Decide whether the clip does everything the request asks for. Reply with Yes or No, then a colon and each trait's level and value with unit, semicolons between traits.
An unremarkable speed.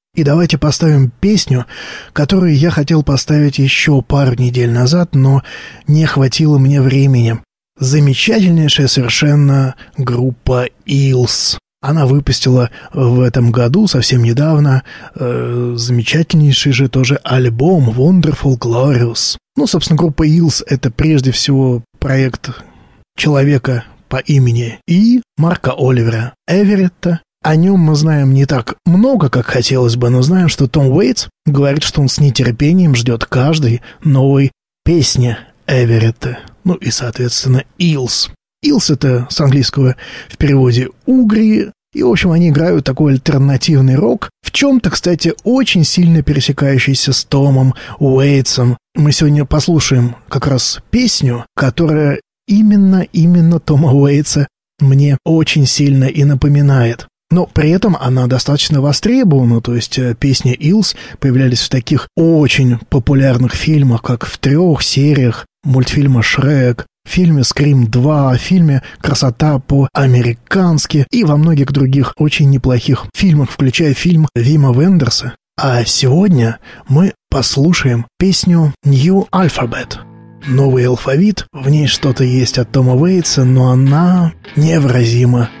Yes: average, 125 wpm